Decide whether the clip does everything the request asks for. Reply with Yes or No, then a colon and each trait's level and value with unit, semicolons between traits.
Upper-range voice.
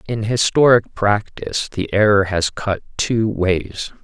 No: low, 105 Hz